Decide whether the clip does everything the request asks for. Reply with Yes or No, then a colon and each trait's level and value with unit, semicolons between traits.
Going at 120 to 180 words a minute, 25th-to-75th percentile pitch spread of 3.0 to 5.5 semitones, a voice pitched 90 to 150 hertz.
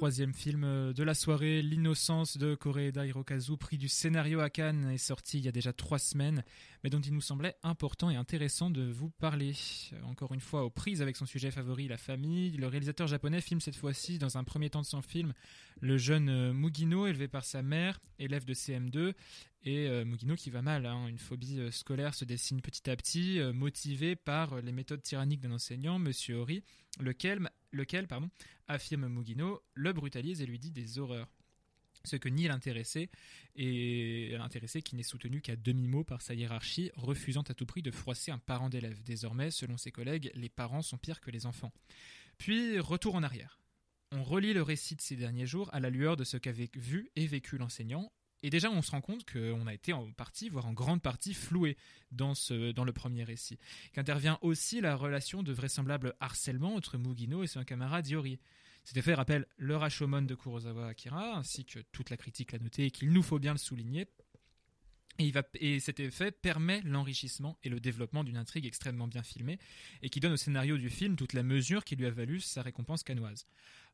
No: average, 200 wpm; average, 3.7 semitones; medium, 140 Hz